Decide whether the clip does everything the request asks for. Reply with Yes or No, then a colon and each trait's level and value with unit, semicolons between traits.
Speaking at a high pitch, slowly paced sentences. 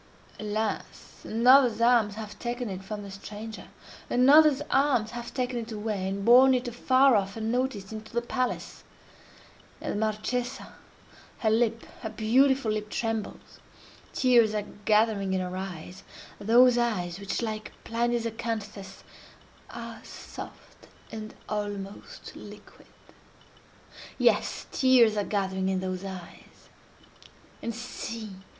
Yes: high, 220 Hz; slow, 115 wpm